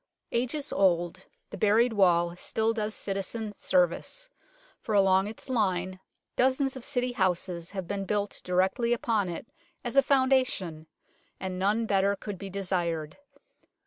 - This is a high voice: Yes, high, 200 Hz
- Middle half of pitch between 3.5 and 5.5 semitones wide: Yes, average, 4.1 semitones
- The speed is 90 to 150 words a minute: Yes, average, 140 wpm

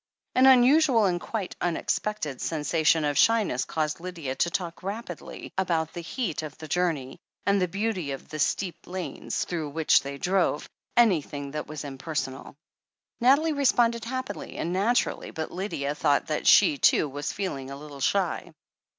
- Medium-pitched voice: Yes, medium, 170 Hz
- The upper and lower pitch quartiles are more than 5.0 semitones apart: Yes, wide, 5.6 semitones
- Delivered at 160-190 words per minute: Yes, average, 165 wpm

